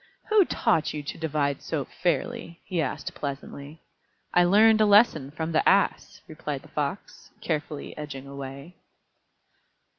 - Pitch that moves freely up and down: No, average, 4.1 semitones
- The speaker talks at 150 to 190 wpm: No, average, 140 wpm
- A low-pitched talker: No, medium, 155 Hz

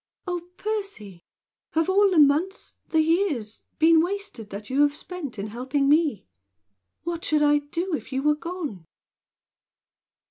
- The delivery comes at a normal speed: Yes, average, 145 wpm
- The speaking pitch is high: Yes, very high, 310 Hz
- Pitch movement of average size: Yes, average, 4.9 semitones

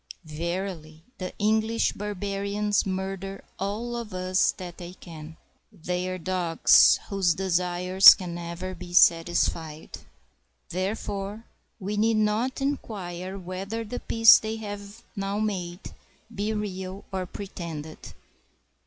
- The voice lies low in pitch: No, high, 190 Hz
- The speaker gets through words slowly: Yes, slow, 115 wpm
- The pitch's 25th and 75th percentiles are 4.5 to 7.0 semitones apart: No, average, 2.8 semitones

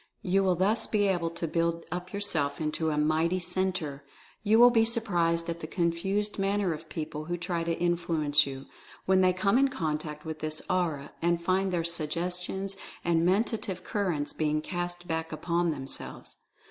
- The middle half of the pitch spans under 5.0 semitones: Yes, average, 2.9 semitones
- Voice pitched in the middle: Yes, medium, 170 Hz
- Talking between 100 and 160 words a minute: No, average, 175 wpm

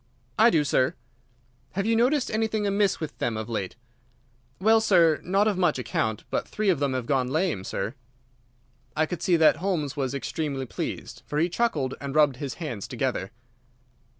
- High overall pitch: No, medium, 155 Hz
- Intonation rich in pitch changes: Yes, wide, 6.9 semitones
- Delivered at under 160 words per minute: No, average, 180 wpm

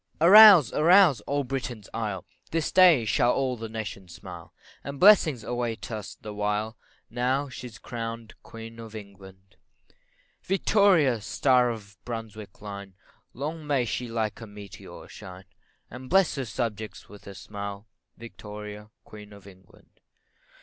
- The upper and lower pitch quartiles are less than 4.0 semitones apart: No, average, 4.3 semitones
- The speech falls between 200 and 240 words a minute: No, average, 145 wpm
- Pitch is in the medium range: No, low, 115 Hz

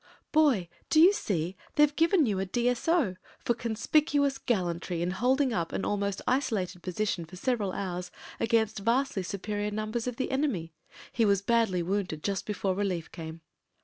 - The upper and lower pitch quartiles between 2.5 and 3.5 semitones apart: No, average, 5.3 semitones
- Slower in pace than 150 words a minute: No, average, 160 wpm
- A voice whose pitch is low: No, high, 210 Hz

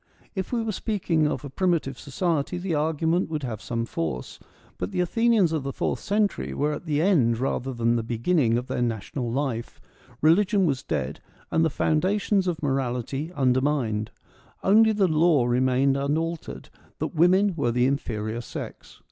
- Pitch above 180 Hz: No, medium, 145 Hz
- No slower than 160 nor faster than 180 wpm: Yes, average, 175 wpm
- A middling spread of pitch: No, wide, 6.3 semitones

